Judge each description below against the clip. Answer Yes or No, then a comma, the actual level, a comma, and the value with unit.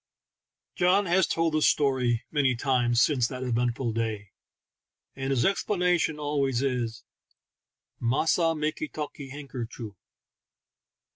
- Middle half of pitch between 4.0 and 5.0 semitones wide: Yes, average, 4.4 semitones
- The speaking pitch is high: No, low, 135 Hz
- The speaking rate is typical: No, slow, 125 wpm